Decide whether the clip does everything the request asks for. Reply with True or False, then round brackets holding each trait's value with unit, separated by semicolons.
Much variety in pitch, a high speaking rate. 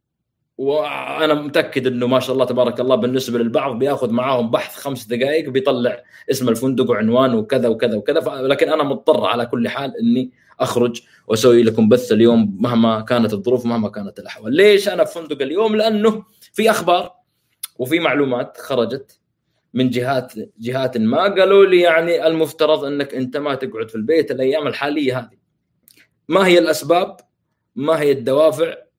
True (6.2 semitones; 155 wpm)